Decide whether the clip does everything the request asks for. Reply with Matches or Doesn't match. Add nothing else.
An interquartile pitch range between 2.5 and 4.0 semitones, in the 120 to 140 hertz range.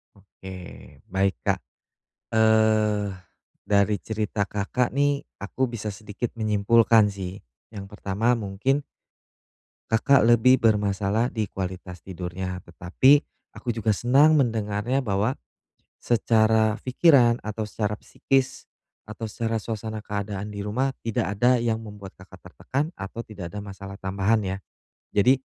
Doesn't match